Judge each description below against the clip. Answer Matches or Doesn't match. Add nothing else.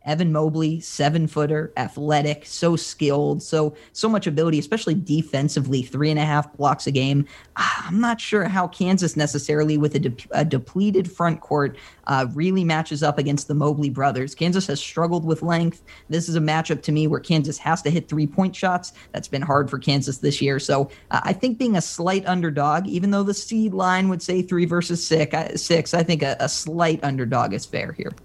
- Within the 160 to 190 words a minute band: Doesn't match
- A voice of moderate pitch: Matches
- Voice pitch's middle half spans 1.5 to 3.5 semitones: Matches